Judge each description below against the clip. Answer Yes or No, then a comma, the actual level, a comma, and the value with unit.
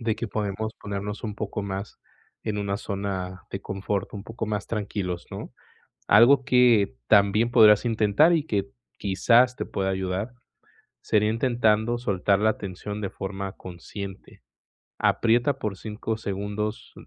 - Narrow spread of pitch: Yes, narrow, 2.3 semitones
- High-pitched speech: No, low, 105 Hz